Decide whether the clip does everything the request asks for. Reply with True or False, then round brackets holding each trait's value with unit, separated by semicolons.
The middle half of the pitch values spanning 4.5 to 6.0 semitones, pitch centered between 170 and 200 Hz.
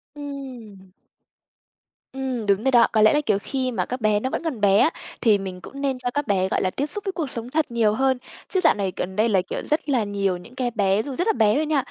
False (5.2 semitones; 240 Hz)